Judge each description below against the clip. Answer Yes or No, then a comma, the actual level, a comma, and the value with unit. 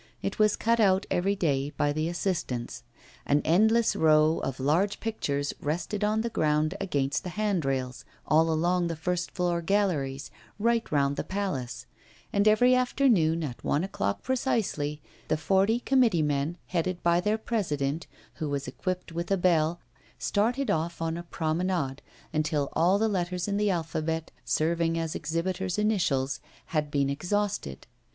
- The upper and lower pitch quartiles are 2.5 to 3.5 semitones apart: No, average, 4.9 semitones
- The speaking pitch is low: No, medium, 170 Hz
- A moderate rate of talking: Yes, average, 155 wpm